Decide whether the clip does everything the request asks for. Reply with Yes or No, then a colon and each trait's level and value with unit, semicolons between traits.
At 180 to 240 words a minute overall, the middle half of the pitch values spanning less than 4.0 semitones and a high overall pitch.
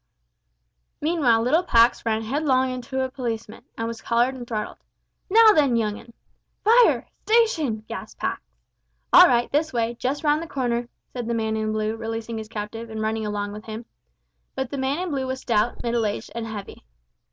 Yes: average, 185 wpm; average, 3.4 semitones; high, 235 Hz